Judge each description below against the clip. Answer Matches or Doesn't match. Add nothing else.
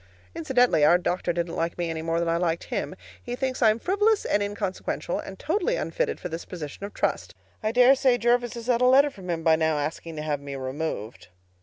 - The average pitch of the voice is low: Doesn't match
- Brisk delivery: Matches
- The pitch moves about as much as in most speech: Doesn't match